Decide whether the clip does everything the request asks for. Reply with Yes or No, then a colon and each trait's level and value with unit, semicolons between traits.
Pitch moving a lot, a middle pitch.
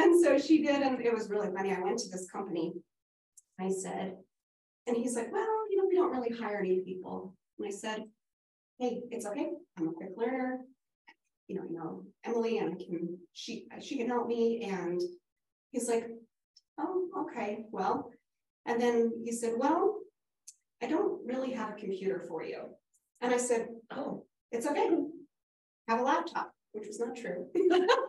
No: wide, 6.2 semitones; high, 235 Hz